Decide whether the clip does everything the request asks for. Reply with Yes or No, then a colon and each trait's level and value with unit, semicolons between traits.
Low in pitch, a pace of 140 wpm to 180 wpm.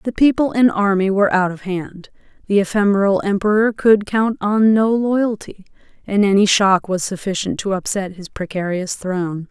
No: high, 200 Hz; average, 165 wpm